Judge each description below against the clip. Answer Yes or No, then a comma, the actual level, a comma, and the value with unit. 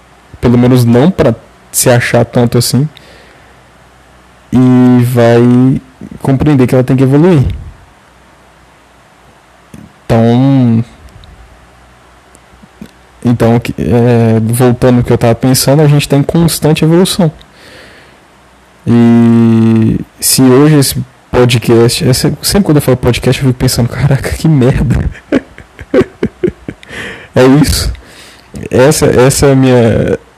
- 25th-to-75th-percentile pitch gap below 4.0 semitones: Yes, average, 2.9 semitones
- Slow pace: Yes, slow, 110 wpm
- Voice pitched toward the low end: Yes, low, 125 Hz